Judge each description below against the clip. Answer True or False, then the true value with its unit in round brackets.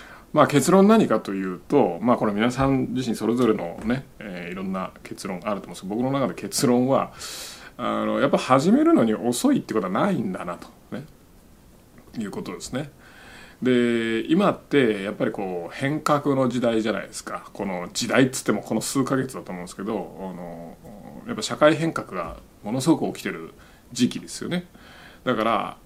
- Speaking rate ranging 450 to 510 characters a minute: False (360 characters per minute)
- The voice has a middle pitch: False (125 Hz)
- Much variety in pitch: False (4.6 semitones)